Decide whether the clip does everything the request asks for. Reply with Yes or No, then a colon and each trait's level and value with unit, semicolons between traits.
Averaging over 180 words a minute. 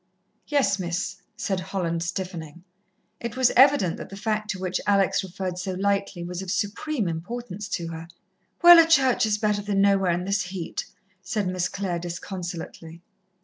No: average, 165 wpm